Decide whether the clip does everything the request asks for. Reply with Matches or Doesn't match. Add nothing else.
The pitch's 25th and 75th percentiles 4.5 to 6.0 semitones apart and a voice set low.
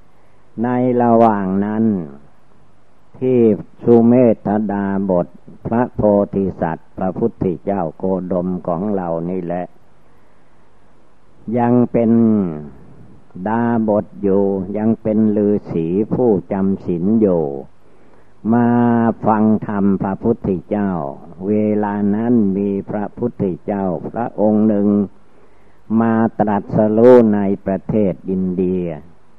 Doesn't match